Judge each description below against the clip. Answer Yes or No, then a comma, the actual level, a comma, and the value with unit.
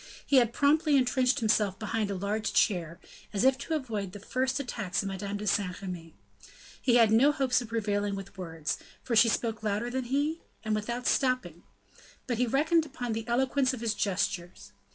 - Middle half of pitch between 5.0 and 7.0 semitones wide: No, average, 4.4 semitones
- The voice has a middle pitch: No, high, 225 Hz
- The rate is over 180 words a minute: Yes, average, 190 wpm